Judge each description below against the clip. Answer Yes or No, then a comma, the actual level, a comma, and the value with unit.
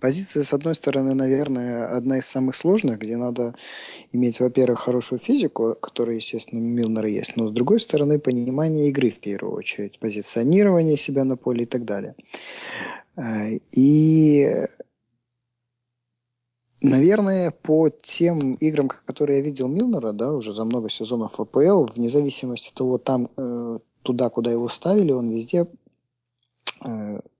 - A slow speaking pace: No, average, 135 wpm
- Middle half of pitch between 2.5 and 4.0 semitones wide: Yes, average, 3.5 semitones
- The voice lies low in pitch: Yes, low, 125 Hz